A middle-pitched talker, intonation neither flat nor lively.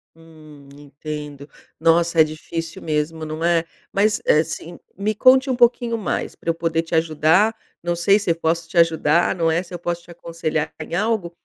No: medium, 165 Hz; narrow, 1.9 semitones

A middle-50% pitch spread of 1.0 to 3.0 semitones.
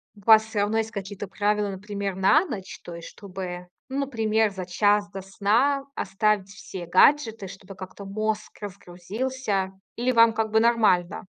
Yes: narrow, 2.5 semitones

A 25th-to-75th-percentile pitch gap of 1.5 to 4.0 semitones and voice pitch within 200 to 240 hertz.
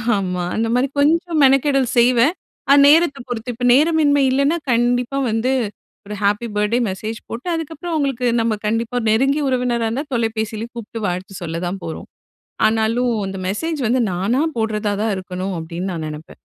No: average, 4.7 semitones; high, 235 Hz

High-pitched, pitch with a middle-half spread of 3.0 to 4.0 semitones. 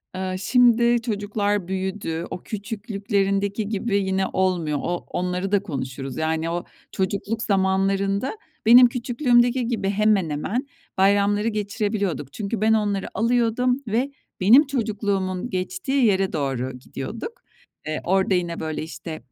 Yes: high, 200 Hz; average, 3.5 semitones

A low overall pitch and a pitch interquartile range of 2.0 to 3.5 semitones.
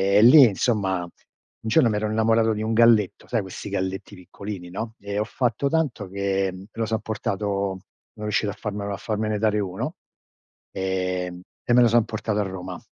Yes: low, 105 Hz; average, 2.8 semitones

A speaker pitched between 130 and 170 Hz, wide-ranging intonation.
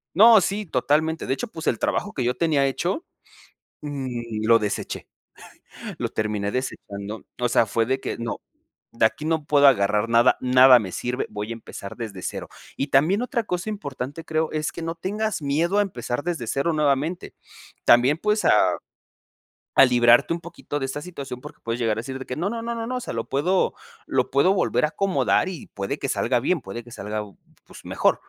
Yes: medium, 140 Hz; wide, 6.3 semitones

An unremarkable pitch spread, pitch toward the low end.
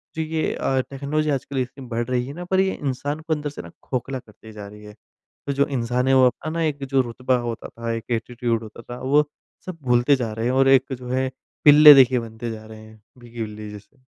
Yes: average, 3.4 semitones; low, 125 Hz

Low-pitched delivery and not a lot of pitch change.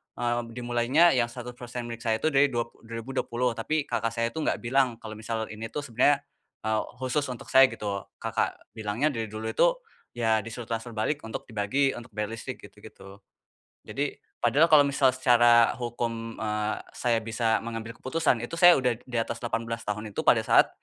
Yes: low, 120 Hz; narrow, 2.3 semitones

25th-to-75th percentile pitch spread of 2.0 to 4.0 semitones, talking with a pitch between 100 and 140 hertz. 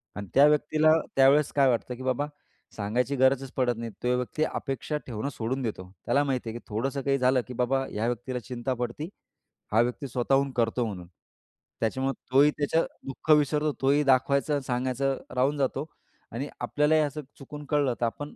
Yes: average, 2.7 semitones; low, 135 Hz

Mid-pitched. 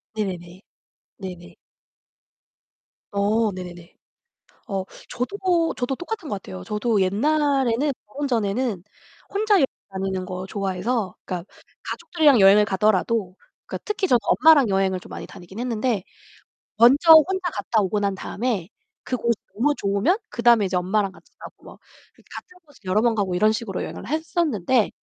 No: high, 215 Hz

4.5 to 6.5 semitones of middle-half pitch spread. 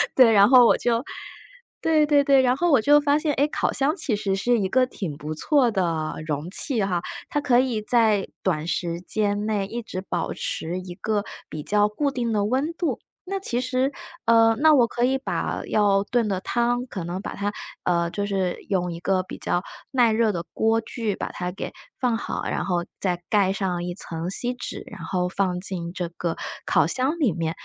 Yes: wide, 5.5 semitones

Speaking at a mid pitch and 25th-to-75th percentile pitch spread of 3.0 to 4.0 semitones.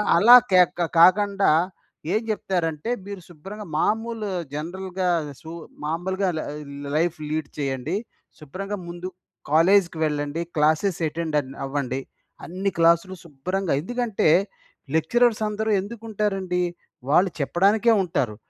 No: medium, 180 Hz; average, 4.4 semitones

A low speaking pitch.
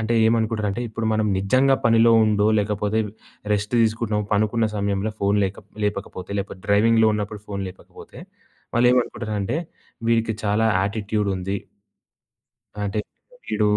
Yes: low, 105 Hz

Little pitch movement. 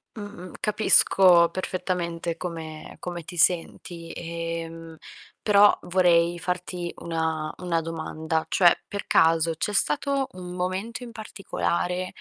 Yes: narrow, 1.8 semitones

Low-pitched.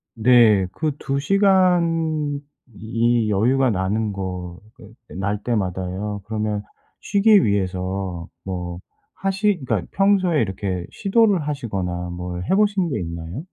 Yes: low, 110 Hz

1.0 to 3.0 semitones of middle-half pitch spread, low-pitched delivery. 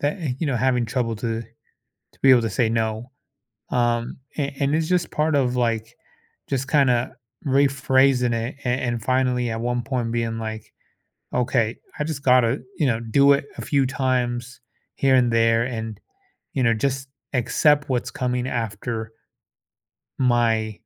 Yes: average, 2.7 semitones; low, 125 Hz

